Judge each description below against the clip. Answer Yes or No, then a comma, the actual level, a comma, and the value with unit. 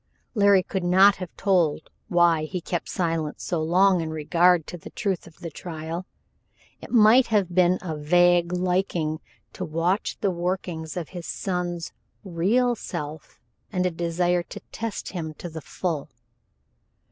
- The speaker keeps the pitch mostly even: Yes, narrow, 2.3 semitones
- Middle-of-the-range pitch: Yes, medium, 175 Hz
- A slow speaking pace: No, average, 155 wpm